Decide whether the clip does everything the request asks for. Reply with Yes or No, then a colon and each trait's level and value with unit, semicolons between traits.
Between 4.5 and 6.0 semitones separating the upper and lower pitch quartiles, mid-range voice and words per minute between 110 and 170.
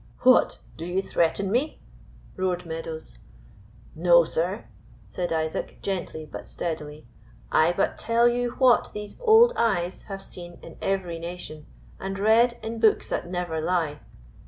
Yes: average, 5.1 semitones; medium, 180 Hz; average, 140 wpm